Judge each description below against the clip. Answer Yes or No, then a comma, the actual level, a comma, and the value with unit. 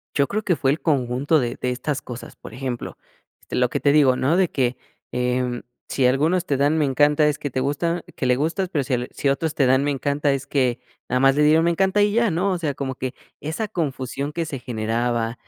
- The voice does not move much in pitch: No, average, 3.8 semitones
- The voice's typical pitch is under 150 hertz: Yes, medium, 140 Hz